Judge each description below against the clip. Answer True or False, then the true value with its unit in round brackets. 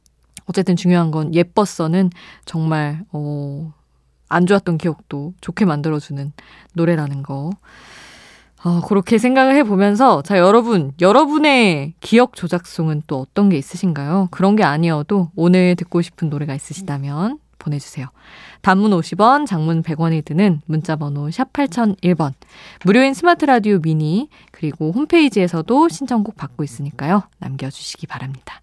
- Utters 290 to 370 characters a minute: True (310 characters per minute)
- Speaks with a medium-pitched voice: True (175 Hz)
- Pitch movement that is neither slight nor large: True (5.0 semitones)